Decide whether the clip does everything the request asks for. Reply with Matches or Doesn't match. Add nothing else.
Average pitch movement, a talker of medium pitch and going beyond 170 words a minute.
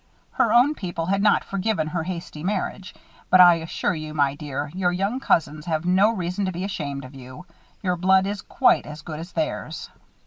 Matches